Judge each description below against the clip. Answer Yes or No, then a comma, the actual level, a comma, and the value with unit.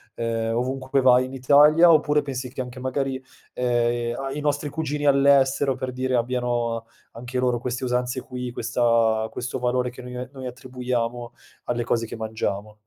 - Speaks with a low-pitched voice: Yes, low, 125 Hz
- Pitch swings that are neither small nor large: No, narrow, 1.9 semitones